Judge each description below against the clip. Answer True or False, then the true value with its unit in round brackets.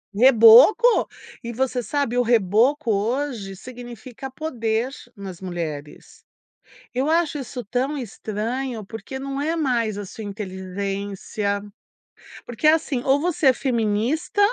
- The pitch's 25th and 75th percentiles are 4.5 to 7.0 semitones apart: True (4.8 semitones)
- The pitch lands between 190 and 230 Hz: False (240 Hz)